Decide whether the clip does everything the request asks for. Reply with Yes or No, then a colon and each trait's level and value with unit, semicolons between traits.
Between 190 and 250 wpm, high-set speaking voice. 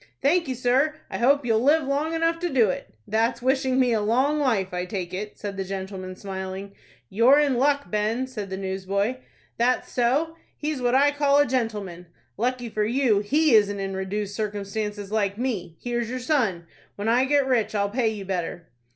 Yes: average, 195 wpm; high, 230 Hz